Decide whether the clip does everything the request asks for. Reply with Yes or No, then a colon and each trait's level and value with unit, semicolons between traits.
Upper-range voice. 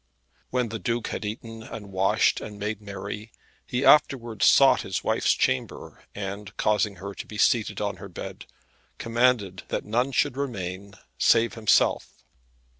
No: low, 105 Hz